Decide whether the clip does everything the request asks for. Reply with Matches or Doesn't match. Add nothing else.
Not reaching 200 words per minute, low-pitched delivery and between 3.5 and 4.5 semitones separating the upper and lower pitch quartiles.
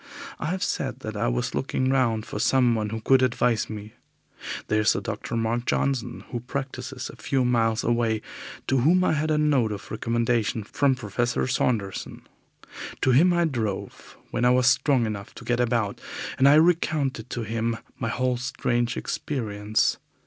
Doesn't match